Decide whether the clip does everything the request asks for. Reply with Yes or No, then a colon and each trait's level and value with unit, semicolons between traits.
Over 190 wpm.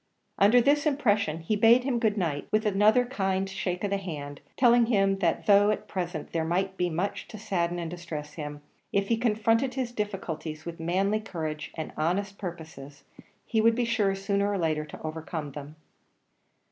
No: average, 185 wpm